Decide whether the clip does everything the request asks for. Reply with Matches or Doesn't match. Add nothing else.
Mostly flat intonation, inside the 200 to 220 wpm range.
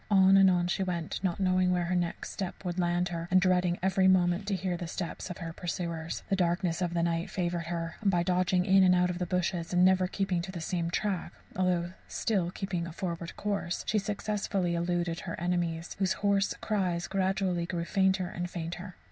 Matches